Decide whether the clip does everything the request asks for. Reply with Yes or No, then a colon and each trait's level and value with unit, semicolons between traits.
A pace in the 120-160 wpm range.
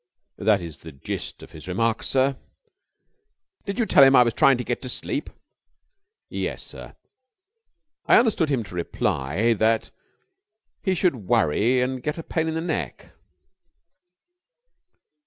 Yes: average, 145 wpm